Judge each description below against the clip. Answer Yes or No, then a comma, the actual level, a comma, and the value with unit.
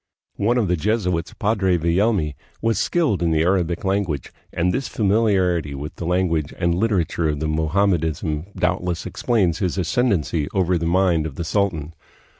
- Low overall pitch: Yes, very low, 90 Hz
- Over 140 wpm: Yes, average, 160 wpm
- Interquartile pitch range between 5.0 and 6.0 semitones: No, average, 3.6 semitones